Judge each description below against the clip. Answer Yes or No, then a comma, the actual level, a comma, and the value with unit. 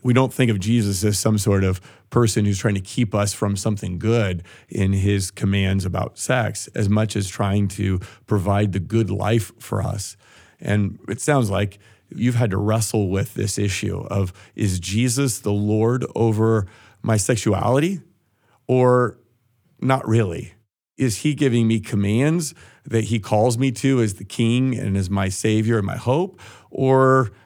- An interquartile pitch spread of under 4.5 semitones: Yes, average, 3.2 semitones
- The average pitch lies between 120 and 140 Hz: No, low, 110 Hz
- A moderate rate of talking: Yes, average, 170 wpm